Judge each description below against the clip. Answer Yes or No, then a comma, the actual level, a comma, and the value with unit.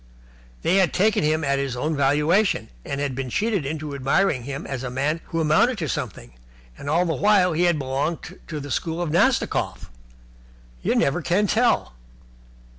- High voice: No, medium, 155 Hz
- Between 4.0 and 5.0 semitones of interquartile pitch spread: Yes, average, 4.4 semitones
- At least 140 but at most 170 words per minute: No, average, 180 wpm